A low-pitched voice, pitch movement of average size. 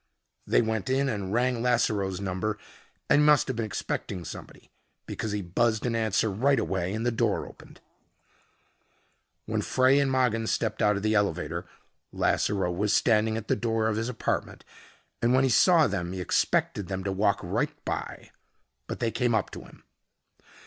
Yes: low, 110 Hz; average, 3.5 semitones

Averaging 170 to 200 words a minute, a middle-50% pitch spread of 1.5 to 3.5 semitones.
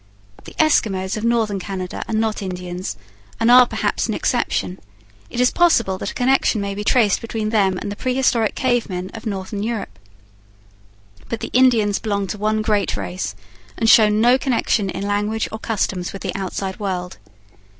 Yes: average, 175 wpm; average, 3.1 semitones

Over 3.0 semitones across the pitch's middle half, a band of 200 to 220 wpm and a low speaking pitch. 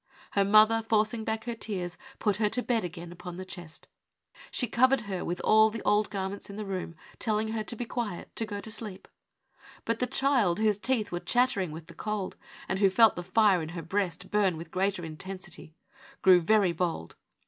No: average, 3.7 semitones; fast, 205 wpm; high, 200 Hz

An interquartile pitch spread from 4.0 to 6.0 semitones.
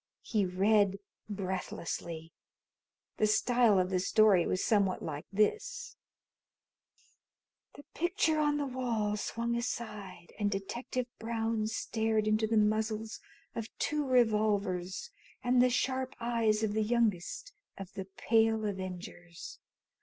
No: average, 3.3 semitones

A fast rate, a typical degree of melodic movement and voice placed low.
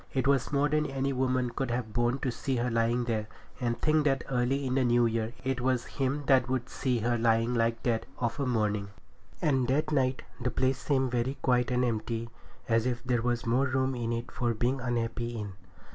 No: fast, 215 wpm; narrow, 2.1 semitones; low, 125 Hz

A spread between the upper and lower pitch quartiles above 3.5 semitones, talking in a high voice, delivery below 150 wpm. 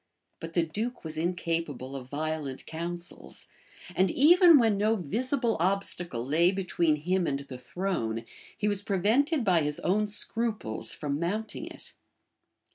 No: wide, 5.6 semitones; medium, 175 Hz; average, 140 wpm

